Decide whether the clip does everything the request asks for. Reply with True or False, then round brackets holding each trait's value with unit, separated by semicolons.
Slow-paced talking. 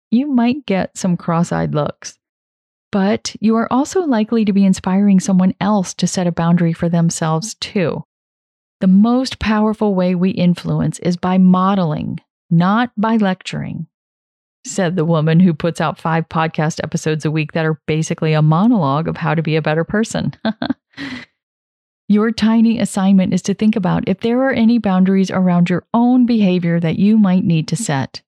False (170 wpm)